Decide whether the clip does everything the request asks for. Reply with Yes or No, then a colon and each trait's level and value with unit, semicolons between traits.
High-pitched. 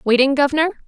Yes: very high, 280 Hz